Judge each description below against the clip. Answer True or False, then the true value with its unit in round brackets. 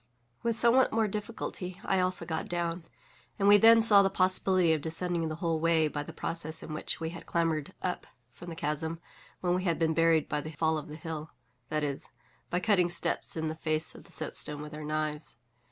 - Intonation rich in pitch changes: False (2.9 semitones)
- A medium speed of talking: False (210 wpm)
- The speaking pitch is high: False (165 Hz)